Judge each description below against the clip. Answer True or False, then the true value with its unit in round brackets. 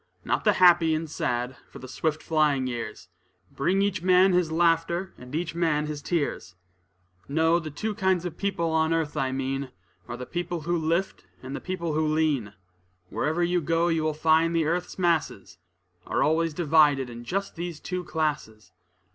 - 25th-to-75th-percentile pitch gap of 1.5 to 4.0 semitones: True (2.9 semitones)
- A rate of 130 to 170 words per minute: False (180 wpm)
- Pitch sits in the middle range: True (160 Hz)